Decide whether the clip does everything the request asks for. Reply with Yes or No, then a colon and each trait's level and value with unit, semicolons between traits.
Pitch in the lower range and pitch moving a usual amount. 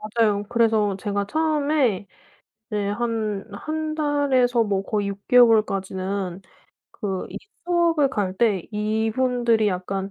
No: high, 215 Hz; average, 3.9 semitones